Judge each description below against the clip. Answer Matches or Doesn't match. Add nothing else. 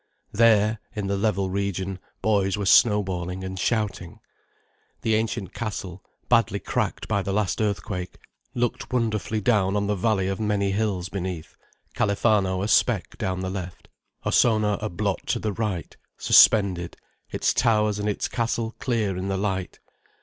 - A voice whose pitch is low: Matches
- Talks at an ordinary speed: Matches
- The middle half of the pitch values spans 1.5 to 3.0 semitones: Matches